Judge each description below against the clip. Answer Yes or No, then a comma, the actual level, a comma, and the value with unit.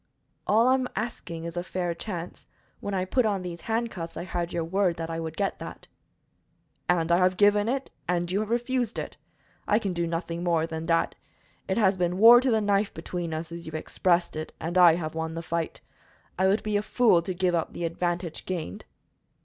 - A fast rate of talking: Yes, fast, 215 wpm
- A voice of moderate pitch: Yes, medium, 180 Hz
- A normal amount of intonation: Yes, average, 3.5 semitones